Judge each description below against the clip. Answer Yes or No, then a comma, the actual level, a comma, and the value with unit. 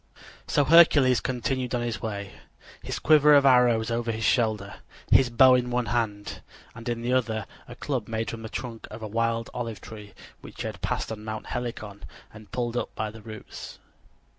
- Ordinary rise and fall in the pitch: No, narrow, 2.1 semitones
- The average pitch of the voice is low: Yes, low, 115 Hz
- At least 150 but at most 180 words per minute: No, average, 190 wpm